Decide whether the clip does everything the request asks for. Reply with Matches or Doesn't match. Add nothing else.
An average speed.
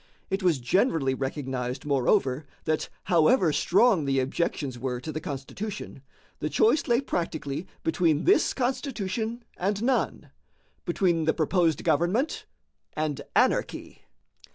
Doesn't match